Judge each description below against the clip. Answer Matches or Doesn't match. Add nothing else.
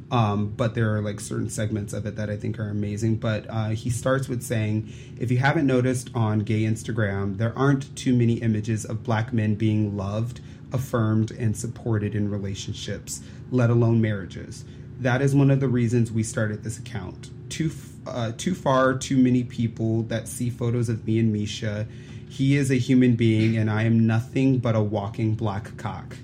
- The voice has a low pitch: Matches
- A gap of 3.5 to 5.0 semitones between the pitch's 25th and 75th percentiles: Doesn't match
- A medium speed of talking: Matches